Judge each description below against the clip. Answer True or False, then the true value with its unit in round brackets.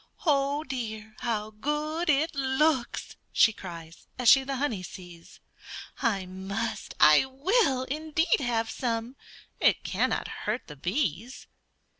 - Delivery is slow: True (125 wpm)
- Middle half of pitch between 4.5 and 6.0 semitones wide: True (5.0 semitones)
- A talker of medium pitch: False (245 Hz)